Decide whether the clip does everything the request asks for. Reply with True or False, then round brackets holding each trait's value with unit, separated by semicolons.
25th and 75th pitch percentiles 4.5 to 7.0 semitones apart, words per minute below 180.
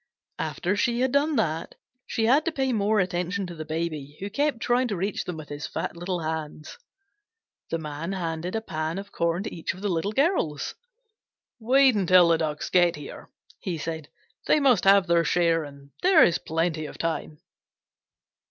False (5.3 semitones; 185 wpm)